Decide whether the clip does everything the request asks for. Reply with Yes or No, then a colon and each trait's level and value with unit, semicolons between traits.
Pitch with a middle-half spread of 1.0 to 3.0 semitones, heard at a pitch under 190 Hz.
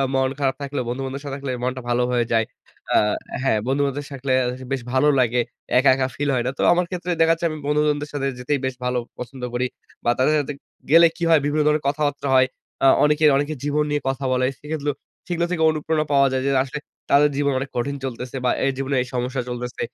Yes: narrow, 2.4 semitones; medium, 140 Hz